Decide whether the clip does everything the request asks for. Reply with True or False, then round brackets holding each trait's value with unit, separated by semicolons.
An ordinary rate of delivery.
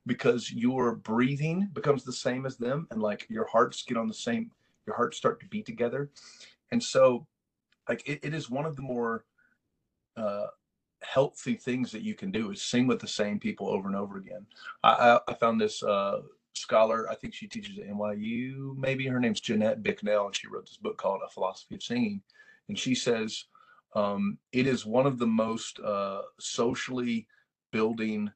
True (190 wpm)